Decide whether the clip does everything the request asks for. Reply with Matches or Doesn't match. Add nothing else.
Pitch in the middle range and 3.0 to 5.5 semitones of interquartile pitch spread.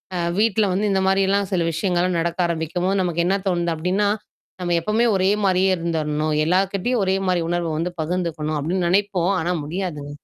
Doesn't match